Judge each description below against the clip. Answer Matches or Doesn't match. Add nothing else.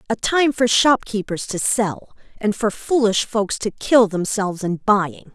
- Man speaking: Doesn't match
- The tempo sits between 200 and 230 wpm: Doesn't match